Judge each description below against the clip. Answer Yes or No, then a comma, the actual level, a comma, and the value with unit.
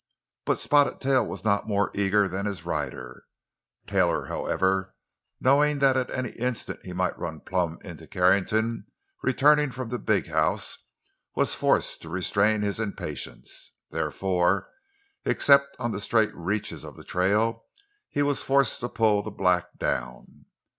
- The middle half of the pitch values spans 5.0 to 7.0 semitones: Yes, average, 5.3 semitones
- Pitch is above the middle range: No, low, 105 Hz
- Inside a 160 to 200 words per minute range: No, average, 145 wpm